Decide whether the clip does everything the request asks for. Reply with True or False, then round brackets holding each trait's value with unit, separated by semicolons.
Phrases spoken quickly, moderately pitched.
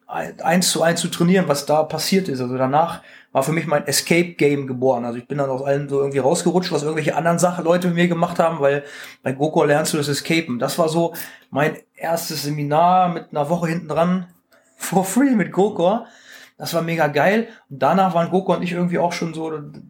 True (215 wpm; 165 Hz)